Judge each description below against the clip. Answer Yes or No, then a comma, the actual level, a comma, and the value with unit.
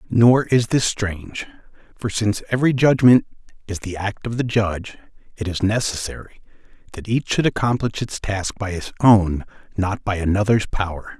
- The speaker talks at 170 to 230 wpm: No, average, 160 wpm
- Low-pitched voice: Yes, low, 105 Hz